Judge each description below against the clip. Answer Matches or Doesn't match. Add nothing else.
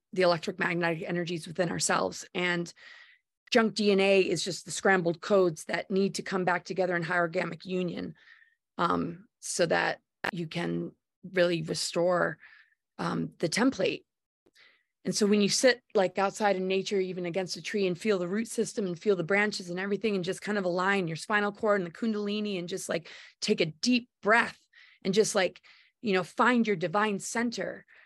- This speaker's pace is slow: Doesn't match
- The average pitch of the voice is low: Doesn't match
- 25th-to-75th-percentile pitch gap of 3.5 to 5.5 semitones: Doesn't match